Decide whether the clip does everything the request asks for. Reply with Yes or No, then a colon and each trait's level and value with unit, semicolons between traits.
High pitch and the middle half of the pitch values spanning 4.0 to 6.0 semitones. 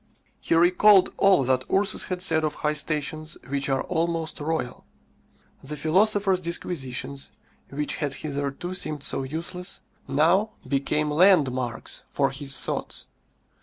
No: medium, 155 Hz; average, 4.5 semitones